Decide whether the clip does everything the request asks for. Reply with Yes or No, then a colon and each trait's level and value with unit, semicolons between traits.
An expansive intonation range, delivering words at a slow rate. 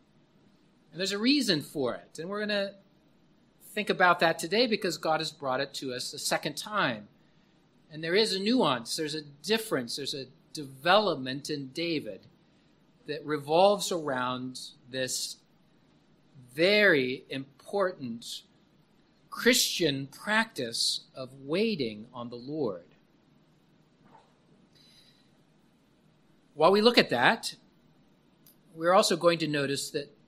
Yes: wide, 6.3 semitones; slow, 120 wpm